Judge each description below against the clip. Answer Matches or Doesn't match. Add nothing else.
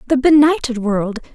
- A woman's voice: Matches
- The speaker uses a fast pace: Doesn't match